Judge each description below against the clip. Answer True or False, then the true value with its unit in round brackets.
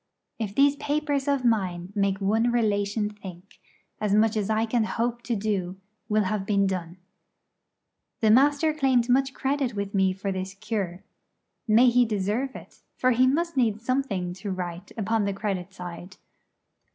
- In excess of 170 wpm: False (165 wpm)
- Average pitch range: True (4.1 semitones)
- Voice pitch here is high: True (215 Hz)